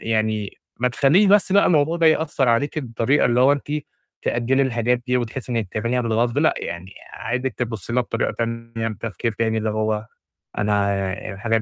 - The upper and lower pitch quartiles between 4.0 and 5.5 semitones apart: No, average, 3.2 semitones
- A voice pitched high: No, low, 115 Hz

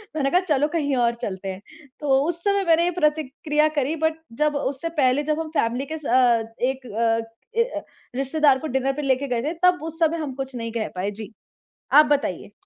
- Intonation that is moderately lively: Yes, average, 3.7 semitones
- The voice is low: No, very high, 285 Hz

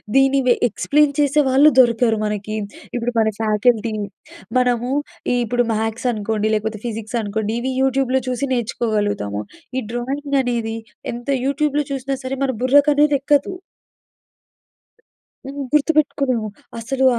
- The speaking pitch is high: Yes, high, 245 Hz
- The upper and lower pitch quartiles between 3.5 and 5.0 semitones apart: Yes, average, 3.8 semitones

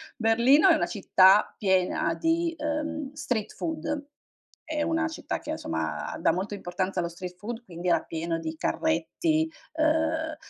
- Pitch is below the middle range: No, very high, 265 Hz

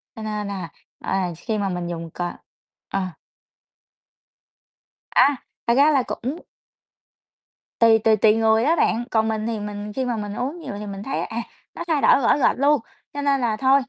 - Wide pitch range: No, average, 4.5 semitones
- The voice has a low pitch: No, high, 225 Hz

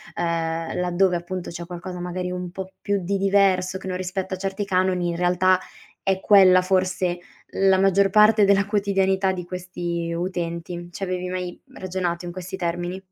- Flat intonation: Yes, narrow, 1.5 semitones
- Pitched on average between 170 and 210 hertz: Yes, medium, 185 Hz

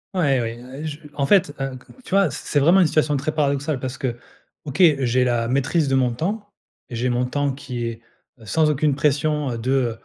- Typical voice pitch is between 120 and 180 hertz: Yes, medium, 140 Hz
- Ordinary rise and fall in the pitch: Yes, average, 3.4 semitones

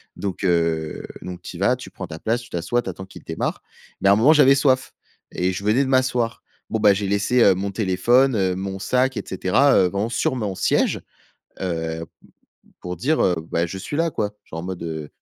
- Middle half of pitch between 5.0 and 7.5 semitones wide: Yes, average, 5.3 semitones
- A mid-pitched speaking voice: No, low, 100 Hz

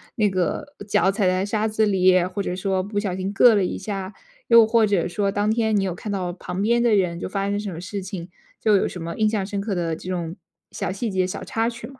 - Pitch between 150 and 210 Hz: Yes, high, 195 Hz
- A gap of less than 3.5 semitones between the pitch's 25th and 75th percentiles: Yes, narrow, 2.6 semitones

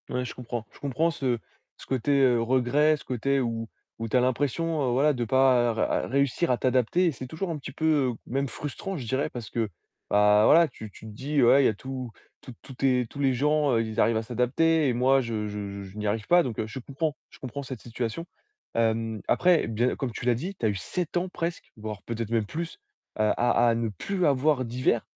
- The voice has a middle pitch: No, low, 125 Hz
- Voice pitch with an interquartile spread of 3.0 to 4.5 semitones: Yes, average, 4.0 semitones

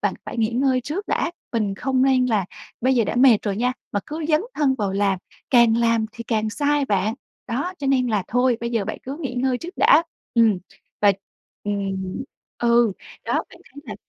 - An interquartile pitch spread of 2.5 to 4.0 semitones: Yes, average, 3.6 semitones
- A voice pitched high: Yes, high, 235 Hz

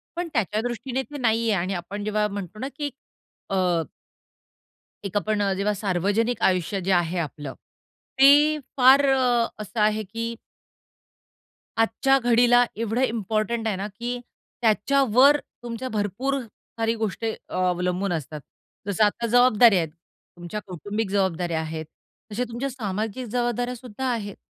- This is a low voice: No, high, 215 Hz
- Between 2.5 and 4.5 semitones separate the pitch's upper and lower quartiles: Yes, average, 3.7 semitones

